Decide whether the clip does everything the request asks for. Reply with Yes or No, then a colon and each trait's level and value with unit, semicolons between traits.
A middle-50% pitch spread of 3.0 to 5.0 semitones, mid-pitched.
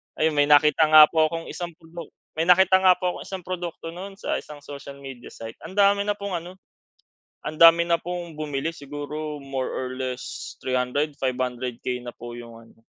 Yes: average, 4.4 semitones; medium, 155 Hz